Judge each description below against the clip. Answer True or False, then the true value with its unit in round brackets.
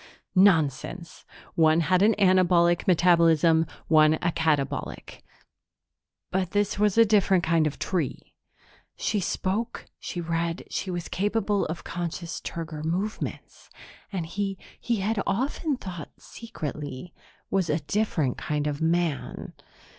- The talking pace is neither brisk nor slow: False (125 wpm)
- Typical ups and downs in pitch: True (3.5 semitones)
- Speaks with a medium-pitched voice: True (175 Hz)